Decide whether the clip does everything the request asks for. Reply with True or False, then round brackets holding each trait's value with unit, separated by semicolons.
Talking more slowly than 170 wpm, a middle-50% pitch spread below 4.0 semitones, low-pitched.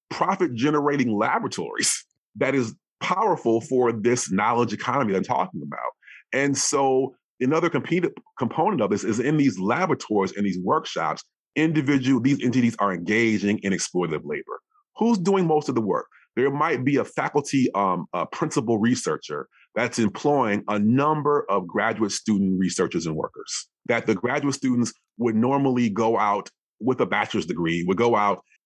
False (160 wpm; 5.1 semitones; 125 Hz)